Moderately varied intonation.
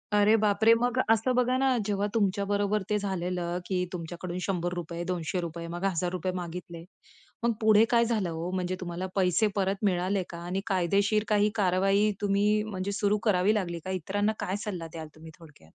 Yes: average, 3.0 semitones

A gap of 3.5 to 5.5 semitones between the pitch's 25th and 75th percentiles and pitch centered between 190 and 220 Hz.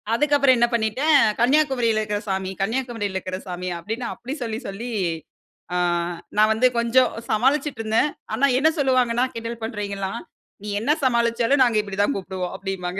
No: average, 4.0 semitones; high, 230 Hz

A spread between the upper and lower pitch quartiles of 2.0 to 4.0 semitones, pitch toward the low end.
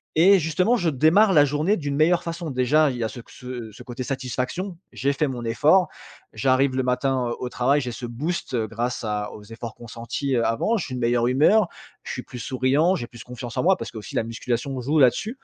No: average, 4.6 semitones; low, 130 Hz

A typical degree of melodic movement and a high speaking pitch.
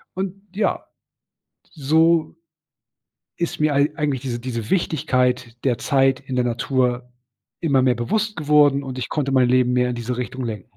No: average, 3.5 semitones; low, 135 Hz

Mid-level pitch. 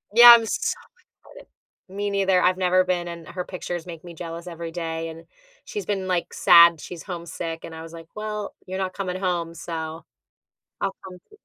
Yes: medium, 175 Hz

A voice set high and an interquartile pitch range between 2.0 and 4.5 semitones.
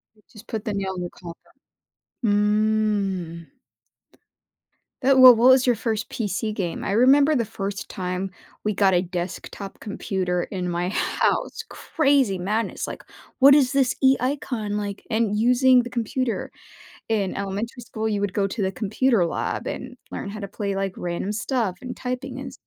Yes: high, 210 Hz; average, 4.1 semitones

